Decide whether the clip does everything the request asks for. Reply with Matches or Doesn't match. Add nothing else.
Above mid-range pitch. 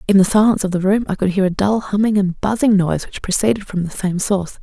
Matches